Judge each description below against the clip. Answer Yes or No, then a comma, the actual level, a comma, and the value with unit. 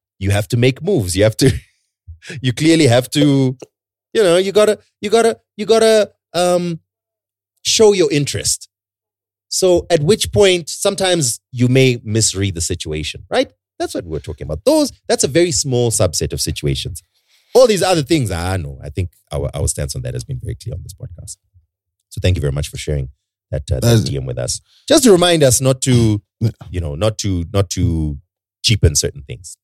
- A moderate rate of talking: Yes, average, 195 wpm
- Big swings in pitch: Yes, wide, 8.8 semitones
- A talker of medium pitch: No, low, 115 Hz